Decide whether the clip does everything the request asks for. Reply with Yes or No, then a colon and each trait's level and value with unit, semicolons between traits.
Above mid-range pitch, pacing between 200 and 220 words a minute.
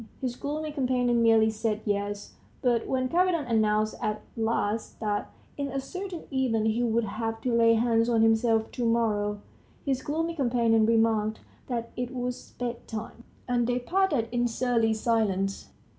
No: high, 230 Hz; average, 155 wpm